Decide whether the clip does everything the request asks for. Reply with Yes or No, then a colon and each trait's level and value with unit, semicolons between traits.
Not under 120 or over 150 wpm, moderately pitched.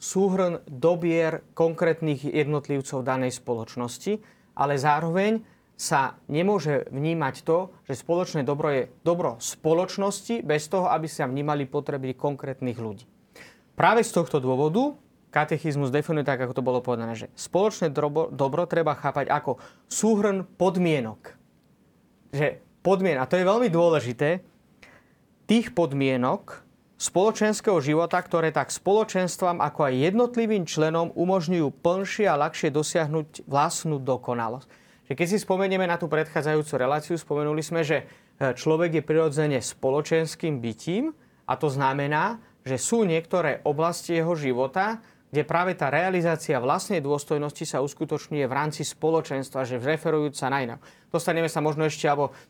Yes: average, 130 wpm; medium, 155 Hz